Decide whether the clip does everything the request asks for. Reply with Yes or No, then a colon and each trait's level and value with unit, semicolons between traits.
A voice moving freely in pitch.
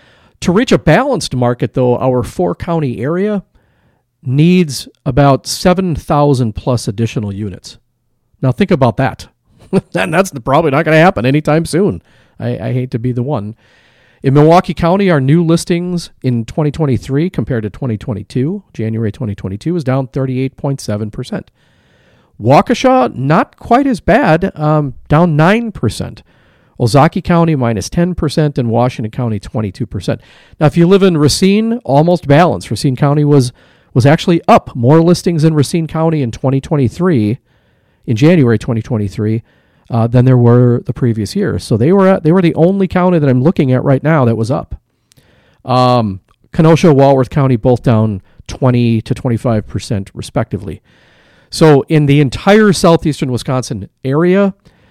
Yes: wide, 5.7 semitones